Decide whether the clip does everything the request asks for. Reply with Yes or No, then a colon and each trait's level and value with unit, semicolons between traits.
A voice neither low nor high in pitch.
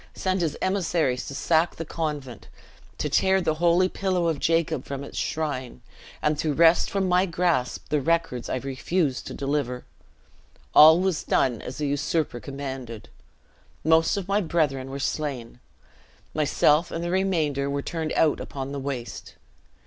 Yes: medium, 155 Hz